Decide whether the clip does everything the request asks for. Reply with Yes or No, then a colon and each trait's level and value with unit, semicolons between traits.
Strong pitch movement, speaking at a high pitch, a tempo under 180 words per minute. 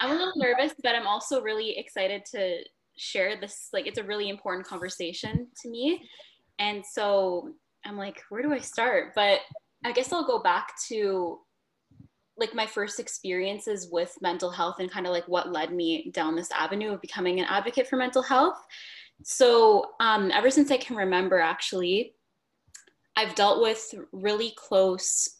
Yes: wide, 6.0 semitones; high, 210 Hz; average, 170 wpm